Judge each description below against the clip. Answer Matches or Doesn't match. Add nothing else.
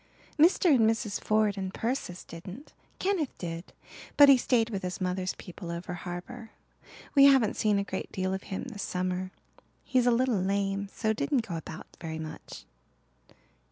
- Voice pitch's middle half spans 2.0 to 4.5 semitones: Doesn't match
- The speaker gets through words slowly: Doesn't match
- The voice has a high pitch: Matches